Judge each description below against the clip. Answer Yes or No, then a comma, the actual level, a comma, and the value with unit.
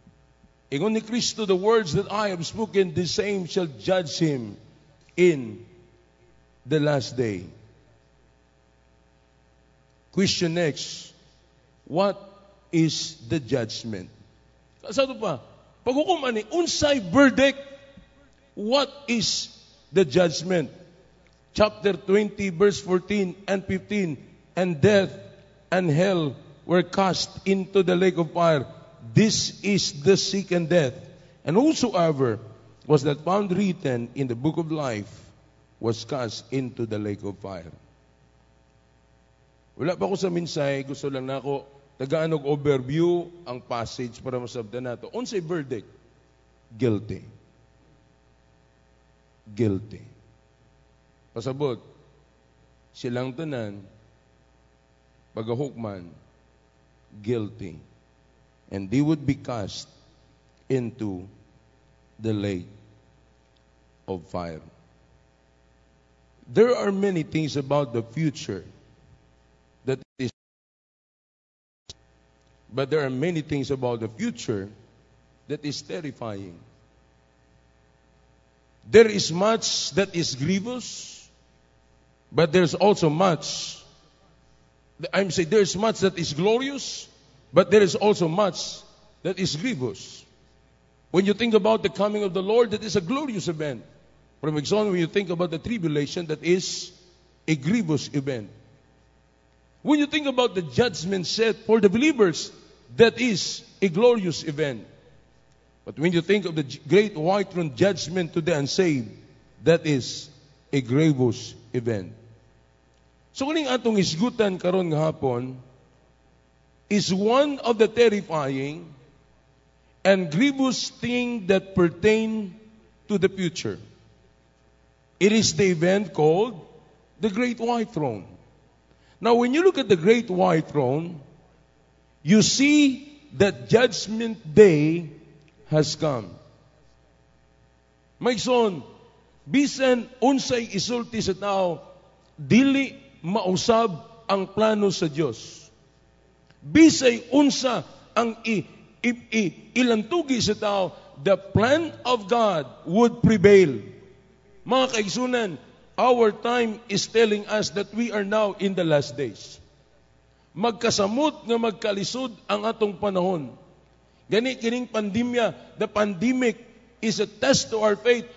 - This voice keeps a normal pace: No, slow, 115 wpm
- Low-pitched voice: No, medium, 170 Hz